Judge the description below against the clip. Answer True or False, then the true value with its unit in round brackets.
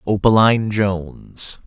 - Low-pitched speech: True (105 Hz)